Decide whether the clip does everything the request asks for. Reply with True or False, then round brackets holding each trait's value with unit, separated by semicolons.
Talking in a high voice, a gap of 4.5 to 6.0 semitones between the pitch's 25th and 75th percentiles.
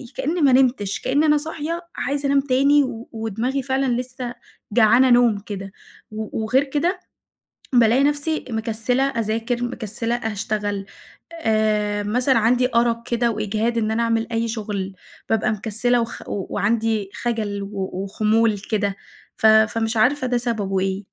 False (230 Hz; 2.9 semitones)